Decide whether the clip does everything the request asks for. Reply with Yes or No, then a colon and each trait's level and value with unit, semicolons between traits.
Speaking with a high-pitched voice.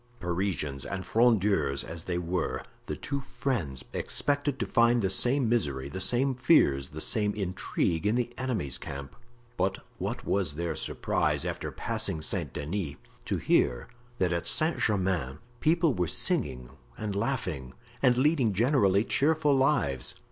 No: low, 100 Hz